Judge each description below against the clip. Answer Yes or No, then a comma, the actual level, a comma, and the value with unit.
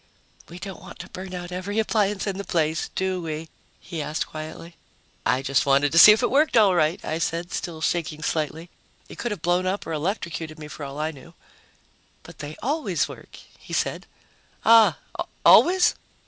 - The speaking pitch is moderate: Yes, medium, 170 Hz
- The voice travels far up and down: No, average, 4.0 semitones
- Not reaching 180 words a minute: No, average, 190 wpm